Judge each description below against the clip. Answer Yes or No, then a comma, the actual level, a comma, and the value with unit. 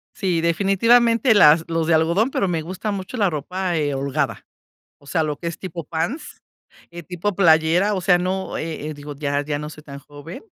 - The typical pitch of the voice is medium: Yes, medium, 170 Hz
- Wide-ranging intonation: No, average, 3.8 semitones